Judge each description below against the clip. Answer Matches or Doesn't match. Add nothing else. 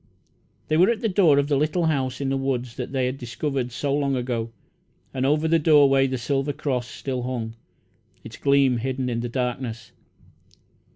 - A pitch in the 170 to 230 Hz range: Doesn't match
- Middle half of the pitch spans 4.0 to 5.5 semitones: Doesn't match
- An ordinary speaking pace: Matches